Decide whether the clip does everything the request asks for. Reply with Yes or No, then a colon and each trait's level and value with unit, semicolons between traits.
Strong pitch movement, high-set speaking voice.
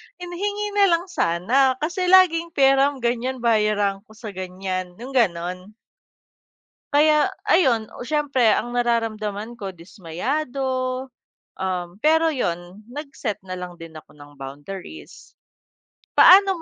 Yes: wide, 7.9 semitones; high, 235 Hz